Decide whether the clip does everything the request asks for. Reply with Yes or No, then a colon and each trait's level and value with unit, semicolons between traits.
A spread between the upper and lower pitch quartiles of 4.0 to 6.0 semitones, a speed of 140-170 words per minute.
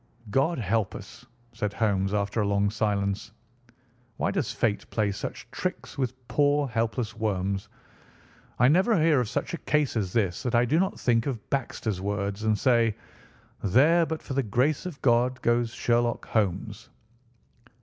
Yes: average, 4.5 semitones; average, 160 wpm